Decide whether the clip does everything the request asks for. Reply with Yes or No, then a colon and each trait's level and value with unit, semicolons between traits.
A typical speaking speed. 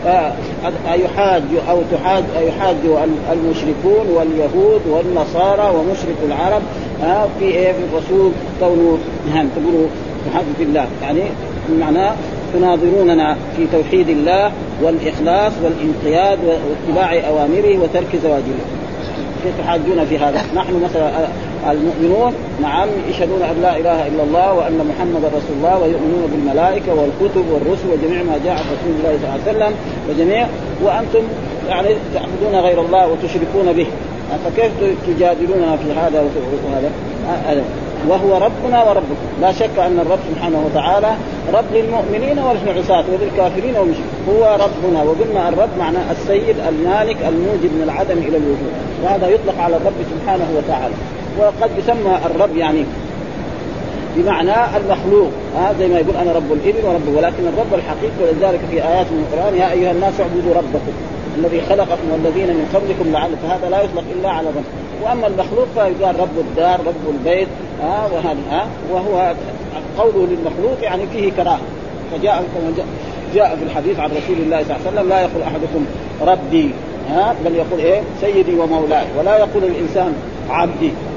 No: fast, 140 wpm